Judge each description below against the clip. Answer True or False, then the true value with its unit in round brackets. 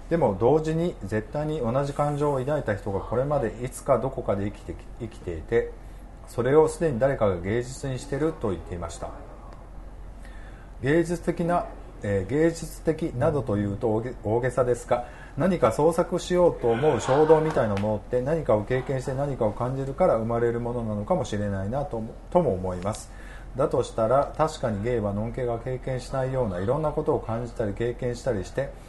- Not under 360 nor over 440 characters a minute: True (380 characters per minute)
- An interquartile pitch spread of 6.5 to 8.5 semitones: False (5.7 semitones)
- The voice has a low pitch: True (125 Hz)